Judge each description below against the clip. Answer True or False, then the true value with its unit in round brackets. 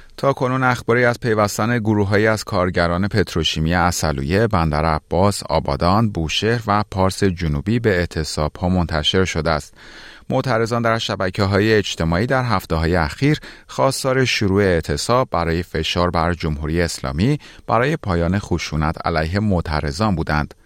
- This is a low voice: True (90 Hz)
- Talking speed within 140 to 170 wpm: False (130 wpm)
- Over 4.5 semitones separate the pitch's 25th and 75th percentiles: True (5.0 semitones)